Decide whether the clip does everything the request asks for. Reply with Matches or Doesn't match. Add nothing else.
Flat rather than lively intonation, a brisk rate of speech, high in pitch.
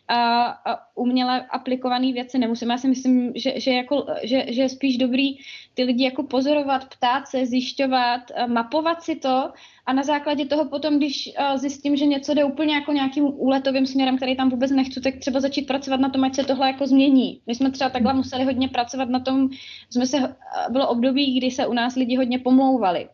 Matches